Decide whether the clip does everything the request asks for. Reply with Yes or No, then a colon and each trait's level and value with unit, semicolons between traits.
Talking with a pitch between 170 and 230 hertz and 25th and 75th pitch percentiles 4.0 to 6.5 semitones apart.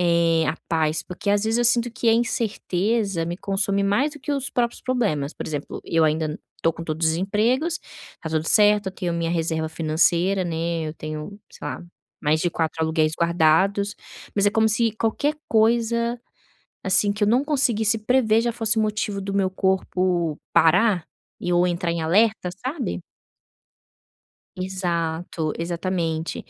Yes: high, 190 Hz; average, 5.0 semitones